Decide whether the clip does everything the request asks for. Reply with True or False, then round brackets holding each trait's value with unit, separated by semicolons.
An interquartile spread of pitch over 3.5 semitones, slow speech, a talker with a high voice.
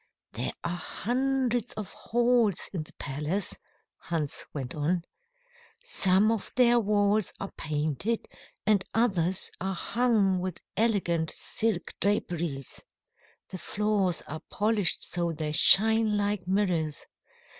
True (4.6 semitones; 115 wpm; 195 Hz)